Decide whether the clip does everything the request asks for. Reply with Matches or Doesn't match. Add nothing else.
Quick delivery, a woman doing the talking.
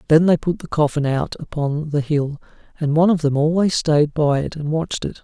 Doesn't match